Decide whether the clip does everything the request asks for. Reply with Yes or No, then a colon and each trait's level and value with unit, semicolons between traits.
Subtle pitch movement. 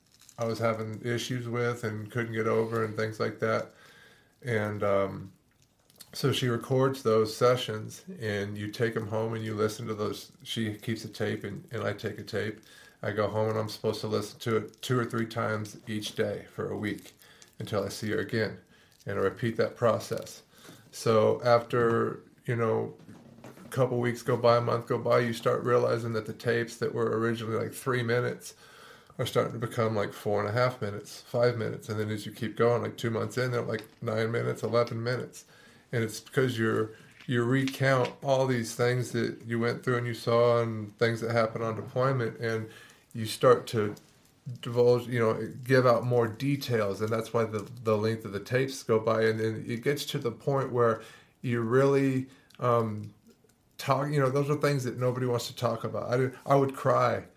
Yes: narrow, 2.2 semitones